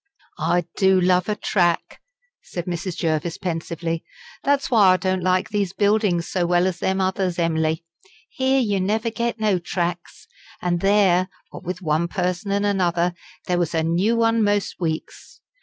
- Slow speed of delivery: No, average, 165 wpm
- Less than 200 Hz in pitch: Yes, medium, 185 Hz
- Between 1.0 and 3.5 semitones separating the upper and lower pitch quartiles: Yes, average, 2.8 semitones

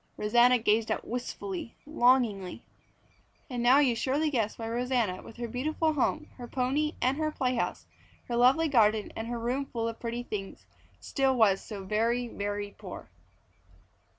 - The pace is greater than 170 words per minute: No, average, 155 wpm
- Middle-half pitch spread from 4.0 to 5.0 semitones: No, average, 3.1 semitones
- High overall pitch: Yes, high, 240 Hz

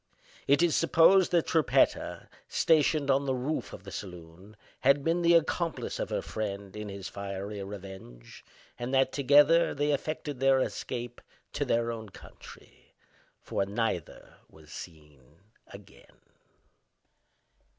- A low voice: Yes, low, 120 Hz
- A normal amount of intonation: No, wide, 6.9 semitones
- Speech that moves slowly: Yes, slow, 130 wpm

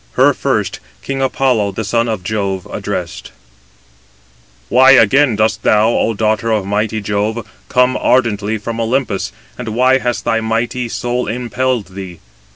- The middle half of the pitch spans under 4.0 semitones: Yes, average, 3.0 semitones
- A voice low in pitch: Yes, low, 115 Hz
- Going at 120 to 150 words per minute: Yes, average, 145 wpm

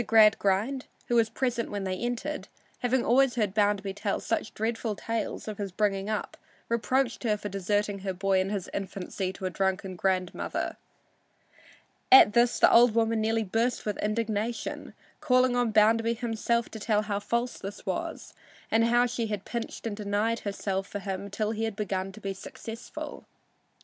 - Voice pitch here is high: Yes, high, 215 Hz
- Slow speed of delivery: No, average, 170 wpm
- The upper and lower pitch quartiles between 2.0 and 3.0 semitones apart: Yes, average, 2.7 semitones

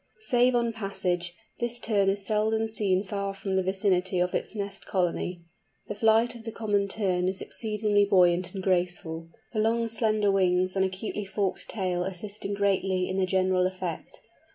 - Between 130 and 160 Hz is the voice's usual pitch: No, high, 195 Hz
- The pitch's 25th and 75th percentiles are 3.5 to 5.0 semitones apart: No, narrow, 2.6 semitones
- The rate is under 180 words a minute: Yes, average, 170 wpm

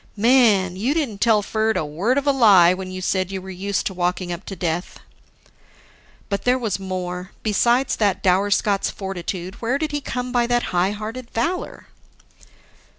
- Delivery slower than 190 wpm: Yes, average, 180 wpm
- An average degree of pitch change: Yes, average, 4.4 semitones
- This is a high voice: Yes, high, 200 Hz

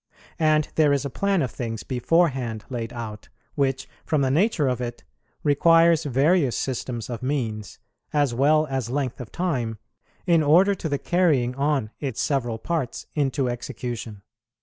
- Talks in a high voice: No, low, 135 Hz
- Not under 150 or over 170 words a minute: Yes, average, 155 wpm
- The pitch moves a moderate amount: Yes, average, 4.2 semitones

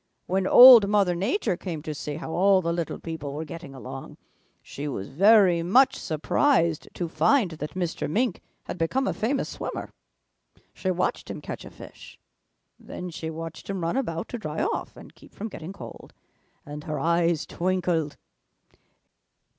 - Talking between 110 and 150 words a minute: No, average, 165 wpm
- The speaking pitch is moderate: Yes, medium, 170 Hz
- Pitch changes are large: No, average, 3.7 semitones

